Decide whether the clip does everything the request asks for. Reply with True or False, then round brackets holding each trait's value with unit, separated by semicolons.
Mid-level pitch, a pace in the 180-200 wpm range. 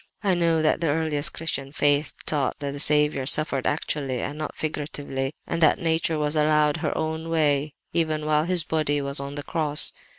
True (150 Hz; 190 wpm)